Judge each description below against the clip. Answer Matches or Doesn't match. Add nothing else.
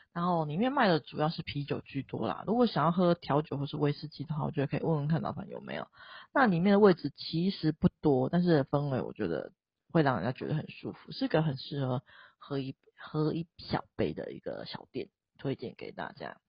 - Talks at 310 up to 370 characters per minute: Matches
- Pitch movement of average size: Matches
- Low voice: Doesn't match